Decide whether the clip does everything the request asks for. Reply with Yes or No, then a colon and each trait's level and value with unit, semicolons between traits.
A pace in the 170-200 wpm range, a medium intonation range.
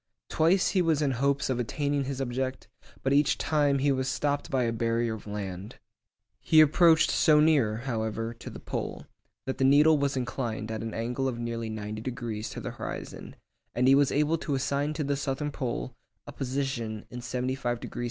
Yes: average, 190 wpm; average, 3.6 semitones